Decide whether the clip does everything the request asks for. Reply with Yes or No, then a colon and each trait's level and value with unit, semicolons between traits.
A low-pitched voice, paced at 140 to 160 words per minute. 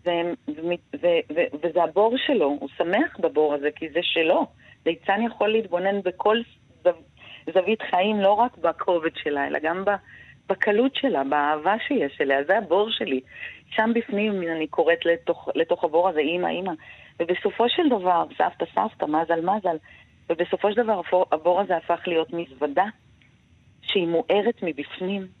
No: medium, 175 Hz; fast, 150 wpm